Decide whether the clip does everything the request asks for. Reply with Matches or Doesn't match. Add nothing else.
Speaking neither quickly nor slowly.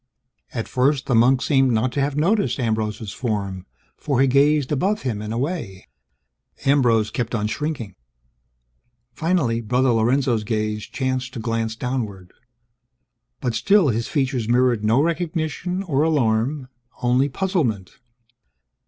Doesn't match